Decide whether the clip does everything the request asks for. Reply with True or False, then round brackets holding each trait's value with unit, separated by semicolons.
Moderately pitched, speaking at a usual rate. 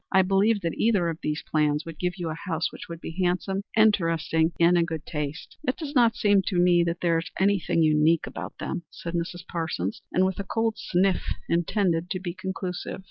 False (175 Hz; 215 wpm)